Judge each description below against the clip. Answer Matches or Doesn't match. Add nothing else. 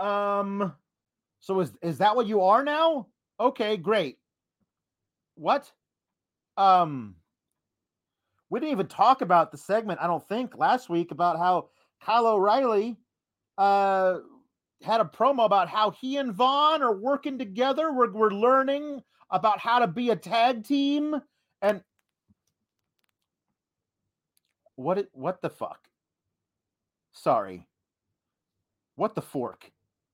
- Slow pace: Matches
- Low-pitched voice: Doesn't match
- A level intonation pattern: Doesn't match